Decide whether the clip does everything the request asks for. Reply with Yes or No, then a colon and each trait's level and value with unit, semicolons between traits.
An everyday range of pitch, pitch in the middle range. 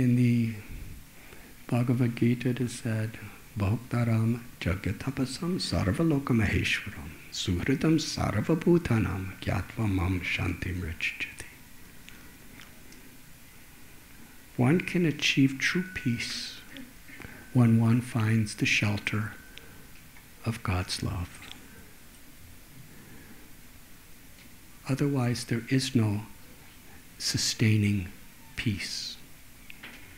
No: average, 4.1 semitones; low, 115 Hz